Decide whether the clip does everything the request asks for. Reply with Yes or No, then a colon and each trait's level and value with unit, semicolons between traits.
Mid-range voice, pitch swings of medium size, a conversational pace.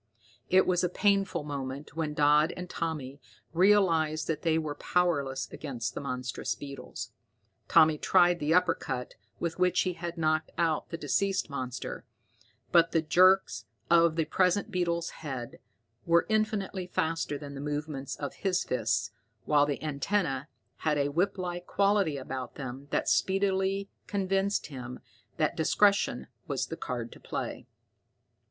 Yes: medium, 160 Hz; average, 4.3 semitones; average, 145 wpm